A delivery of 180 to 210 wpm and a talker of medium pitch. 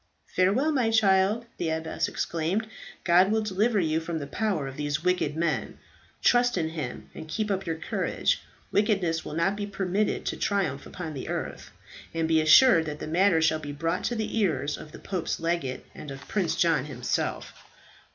Yes: average, 185 wpm; medium, 170 Hz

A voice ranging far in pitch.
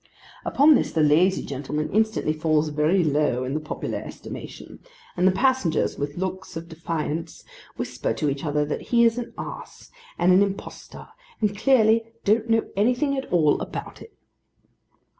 Yes: wide, 6.6 semitones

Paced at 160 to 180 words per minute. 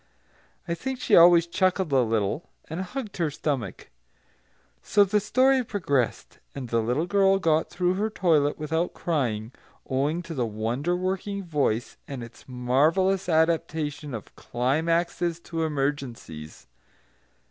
No: slow, 135 wpm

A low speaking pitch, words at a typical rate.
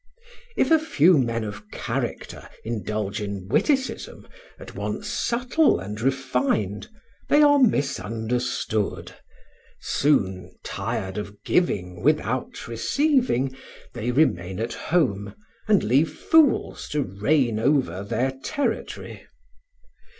No: low, 125 Hz; slow, 105 wpm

